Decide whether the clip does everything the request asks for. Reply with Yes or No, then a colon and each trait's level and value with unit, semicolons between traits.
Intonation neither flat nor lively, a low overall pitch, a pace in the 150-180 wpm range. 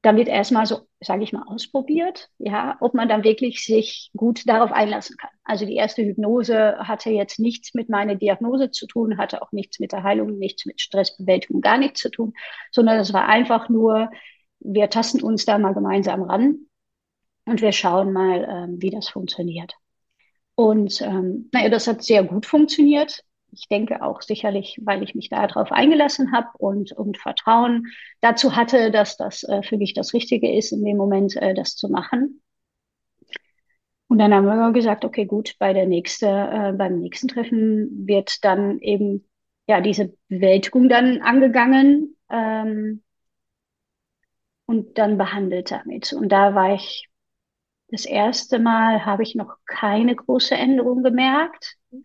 No: average, 3.4 semitones; high, 220 Hz; average, 160 wpm